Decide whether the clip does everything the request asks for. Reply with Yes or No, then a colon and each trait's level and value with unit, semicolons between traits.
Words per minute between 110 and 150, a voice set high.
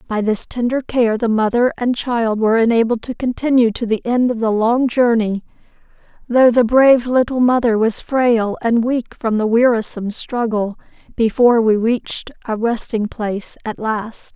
No: average, 165 wpm; high, 230 Hz